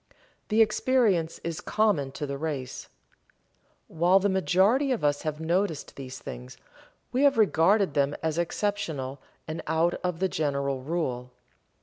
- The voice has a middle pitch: Yes, medium, 165 Hz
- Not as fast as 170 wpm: Yes, average, 140 wpm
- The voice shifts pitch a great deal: Yes, wide, 5.7 semitones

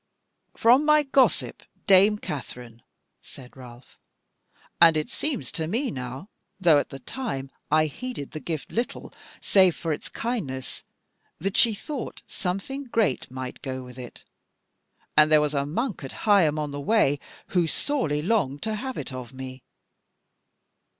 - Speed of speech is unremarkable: Yes, average, 150 wpm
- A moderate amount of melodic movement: No, wide, 8.6 semitones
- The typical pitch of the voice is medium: Yes, medium, 155 Hz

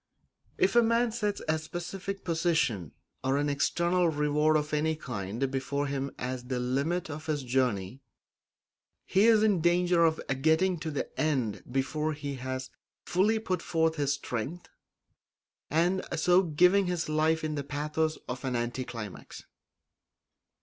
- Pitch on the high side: No, medium, 155 Hz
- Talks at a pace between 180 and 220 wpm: No, average, 145 wpm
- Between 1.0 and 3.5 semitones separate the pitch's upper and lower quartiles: No, average, 4.6 semitones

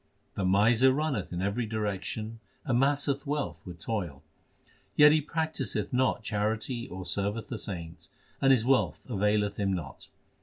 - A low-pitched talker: Yes, low, 110 Hz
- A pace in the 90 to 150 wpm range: Yes, average, 145 wpm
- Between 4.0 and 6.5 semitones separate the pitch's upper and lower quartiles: Yes, average, 5.2 semitones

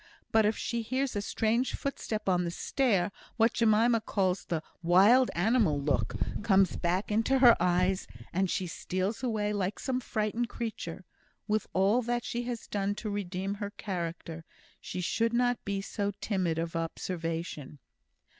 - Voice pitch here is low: No, high, 205 Hz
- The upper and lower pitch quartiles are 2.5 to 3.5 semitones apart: No, average, 4.2 semitones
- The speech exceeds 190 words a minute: No, average, 155 wpm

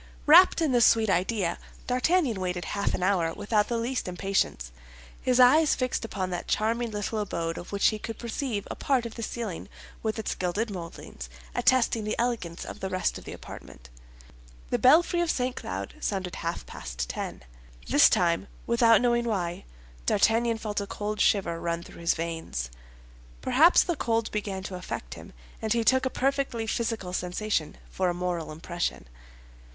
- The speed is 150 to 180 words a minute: Yes, average, 175 wpm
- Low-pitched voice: No, high, 210 Hz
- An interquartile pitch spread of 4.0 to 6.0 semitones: Yes, average, 5.0 semitones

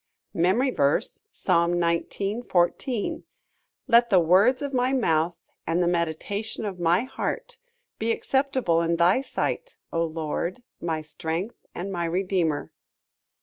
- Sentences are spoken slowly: Yes, slow, 130 wpm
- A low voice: No, medium, 180 Hz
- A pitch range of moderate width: No, wide, 5.8 semitones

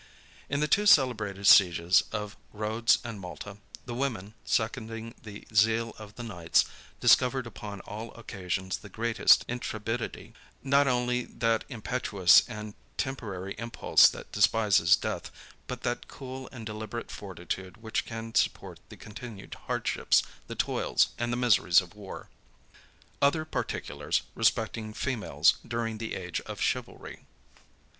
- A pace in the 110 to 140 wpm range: Yes, slow, 135 wpm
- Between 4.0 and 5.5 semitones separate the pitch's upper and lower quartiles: No, average, 2.9 semitones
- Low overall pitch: Yes, low, 110 Hz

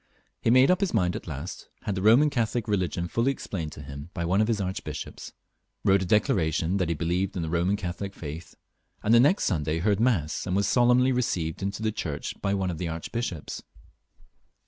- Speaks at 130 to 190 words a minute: No, fast, 205 wpm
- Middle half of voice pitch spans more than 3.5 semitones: Yes, average, 4.9 semitones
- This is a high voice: No, very low, 95 Hz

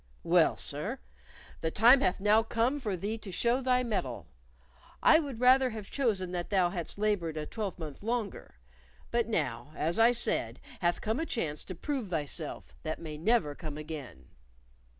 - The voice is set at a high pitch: Yes, high, 200 Hz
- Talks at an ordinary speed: Yes, average, 170 wpm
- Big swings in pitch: Yes, wide, 6.6 semitones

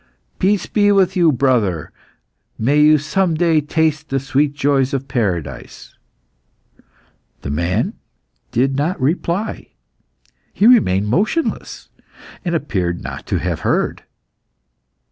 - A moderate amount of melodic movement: No, wide, 5.8 semitones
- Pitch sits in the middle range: Yes, medium, 145 Hz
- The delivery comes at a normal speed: No, slow, 115 wpm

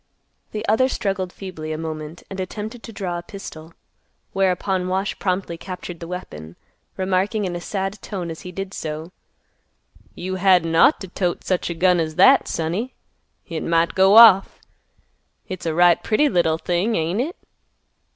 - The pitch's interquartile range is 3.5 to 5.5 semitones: No, average, 2.7 semitones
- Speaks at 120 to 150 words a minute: No, average, 165 wpm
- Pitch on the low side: No, medium, 185 Hz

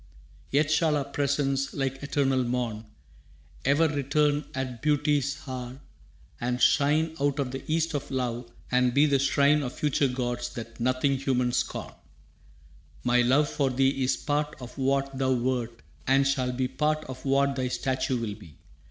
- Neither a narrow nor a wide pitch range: No, narrow, 2.2 semitones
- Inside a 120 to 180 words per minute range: Yes, average, 160 wpm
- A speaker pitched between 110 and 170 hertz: Yes, low, 135 Hz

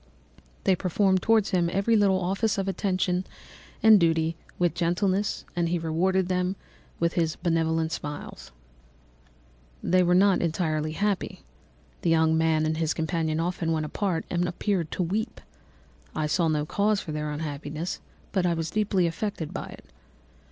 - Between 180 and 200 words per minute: No, average, 155 wpm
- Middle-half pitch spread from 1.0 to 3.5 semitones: Yes, average, 2.9 semitones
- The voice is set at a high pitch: No, medium, 175 Hz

